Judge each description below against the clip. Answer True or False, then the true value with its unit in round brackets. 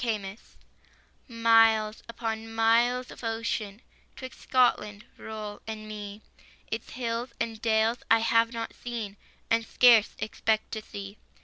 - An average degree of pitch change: False (1.4 semitones)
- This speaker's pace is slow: True (130 wpm)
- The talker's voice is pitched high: True (225 Hz)